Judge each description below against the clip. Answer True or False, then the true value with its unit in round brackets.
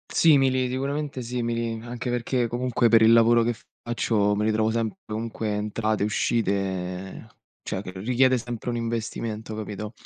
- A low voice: True (115 Hz)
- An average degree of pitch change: False (2.3 semitones)